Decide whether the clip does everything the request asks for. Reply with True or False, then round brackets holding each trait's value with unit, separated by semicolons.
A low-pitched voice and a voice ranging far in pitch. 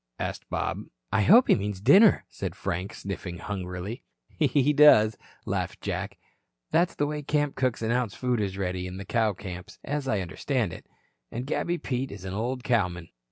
True (110 Hz; 6.4 semitones)